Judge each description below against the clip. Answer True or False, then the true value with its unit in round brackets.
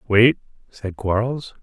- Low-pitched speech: True (110 Hz)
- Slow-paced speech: True (110 wpm)